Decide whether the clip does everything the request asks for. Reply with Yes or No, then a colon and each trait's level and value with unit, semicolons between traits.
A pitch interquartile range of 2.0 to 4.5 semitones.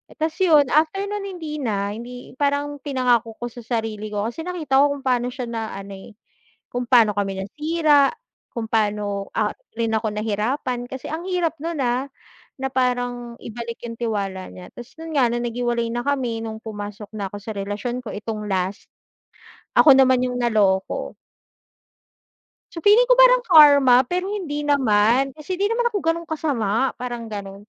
No: average, 5.2 semitones